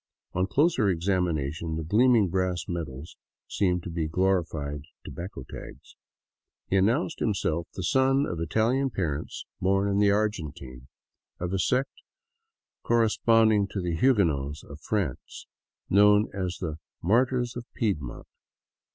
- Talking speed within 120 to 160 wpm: Yes, average, 140 wpm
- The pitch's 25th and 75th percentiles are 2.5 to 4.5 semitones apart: No, average, 5.1 semitones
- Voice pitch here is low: Yes, very low, 95 Hz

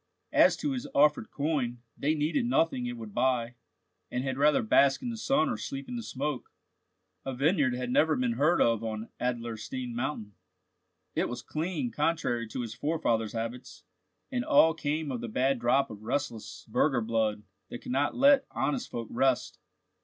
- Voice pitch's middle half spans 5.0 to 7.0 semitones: Yes, average, 5.3 semitones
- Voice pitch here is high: No, low, 130 Hz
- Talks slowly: No, average, 175 wpm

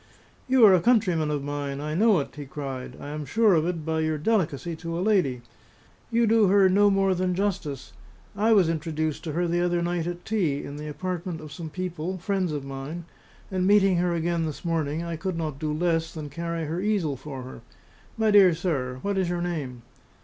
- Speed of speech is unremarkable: No, fast, 215 wpm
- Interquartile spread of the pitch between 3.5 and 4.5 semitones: Yes, average, 3.8 semitones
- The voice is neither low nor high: Yes, medium, 170 Hz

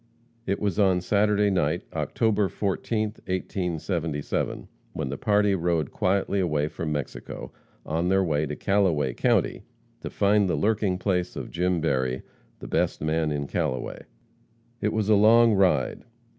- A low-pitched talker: Yes, very low, 90 Hz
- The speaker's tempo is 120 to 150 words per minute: Yes, average, 145 wpm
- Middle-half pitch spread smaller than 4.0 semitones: No, average, 4.6 semitones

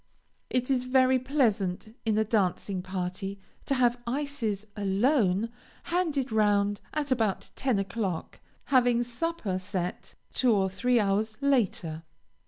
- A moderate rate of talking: No, slow, 125 wpm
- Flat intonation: No, average, 4.6 semitones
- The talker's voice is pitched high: Yes, high, 220 Hz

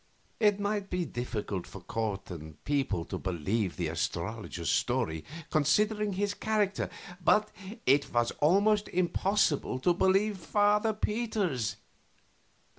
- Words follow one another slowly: Yes, slow, 115 wpm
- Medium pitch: Yes, medium, 170 Hz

